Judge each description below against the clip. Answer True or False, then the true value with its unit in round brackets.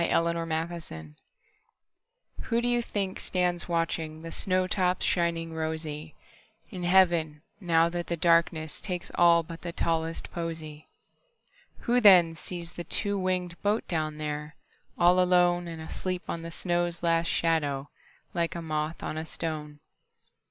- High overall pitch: False (170 Hz)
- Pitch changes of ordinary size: False (1.9 semitones)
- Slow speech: True (125 wpm)